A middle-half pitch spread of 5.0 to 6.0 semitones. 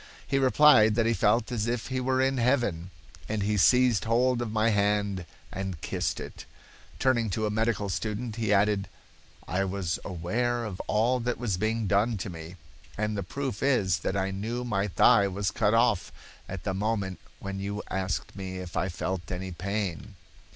No: average, 3.5 semitones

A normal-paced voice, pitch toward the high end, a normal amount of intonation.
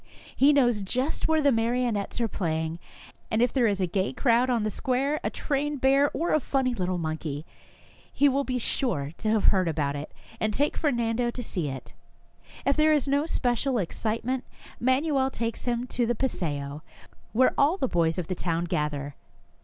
No: average, 185 wpm; high, 235 Hz; wide, 6.9 semitones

